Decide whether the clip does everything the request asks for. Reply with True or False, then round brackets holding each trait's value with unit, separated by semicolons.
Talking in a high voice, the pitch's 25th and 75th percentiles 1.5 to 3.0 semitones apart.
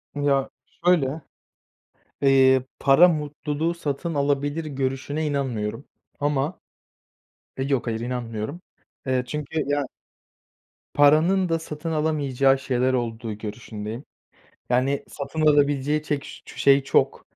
False (140 Hz; 2.6 semitones)